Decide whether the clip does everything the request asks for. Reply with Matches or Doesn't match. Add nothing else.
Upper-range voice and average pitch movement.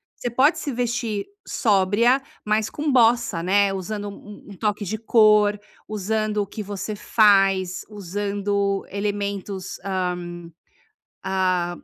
Doesn't match